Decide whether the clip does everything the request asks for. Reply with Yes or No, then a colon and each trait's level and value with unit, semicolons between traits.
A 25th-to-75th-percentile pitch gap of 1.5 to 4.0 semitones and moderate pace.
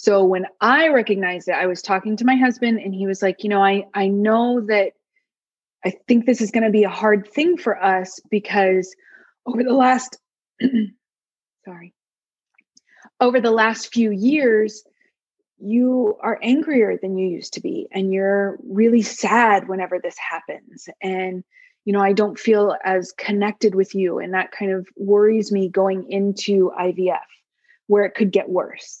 Yes: average, 3.1 semitones; average, 170 wpm